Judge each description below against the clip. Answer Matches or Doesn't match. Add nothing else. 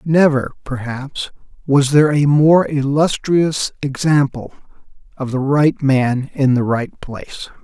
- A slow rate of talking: Matches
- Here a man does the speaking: Matches